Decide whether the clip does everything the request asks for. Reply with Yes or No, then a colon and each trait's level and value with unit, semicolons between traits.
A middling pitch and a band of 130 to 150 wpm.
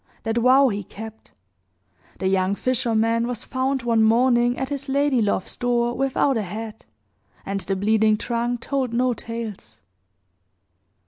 No: high, 235 Hz; average, 140 wpm